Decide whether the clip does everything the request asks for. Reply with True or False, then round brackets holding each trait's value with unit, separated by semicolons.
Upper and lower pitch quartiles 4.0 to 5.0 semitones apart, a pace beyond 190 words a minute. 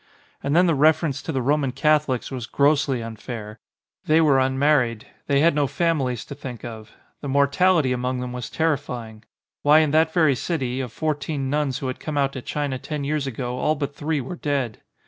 False (3.2 semitones; 200 wpm)